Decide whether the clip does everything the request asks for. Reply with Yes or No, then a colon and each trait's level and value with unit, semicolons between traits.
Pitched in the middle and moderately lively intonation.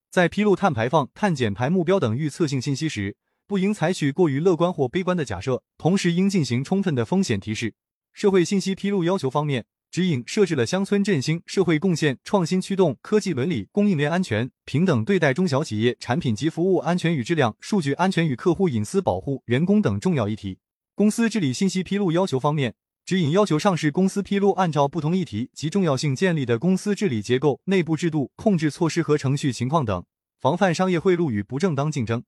No: medium, 170 Hz; wide, 6.1 semitones